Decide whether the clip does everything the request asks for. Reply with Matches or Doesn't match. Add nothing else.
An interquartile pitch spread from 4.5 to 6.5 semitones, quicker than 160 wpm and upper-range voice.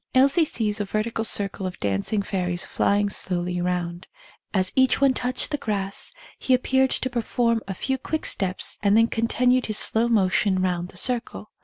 Matches